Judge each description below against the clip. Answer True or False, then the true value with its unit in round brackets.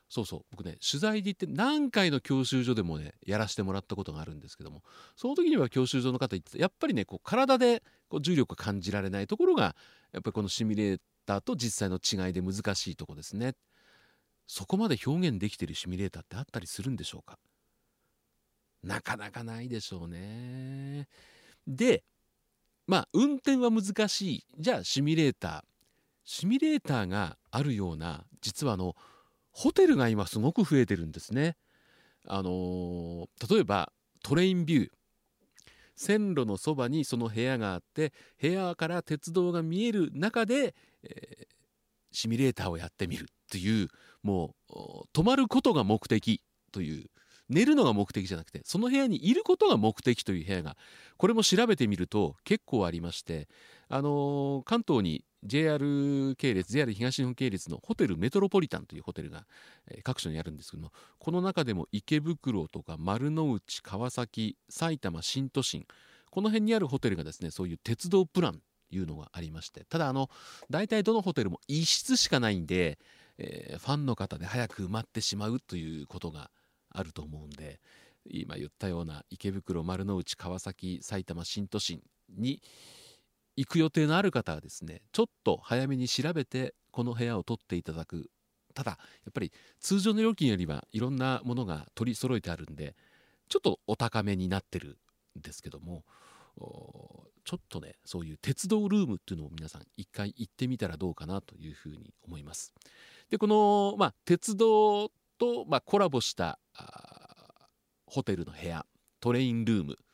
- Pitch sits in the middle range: False (120 Hz)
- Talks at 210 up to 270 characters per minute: False (345 characters per minute)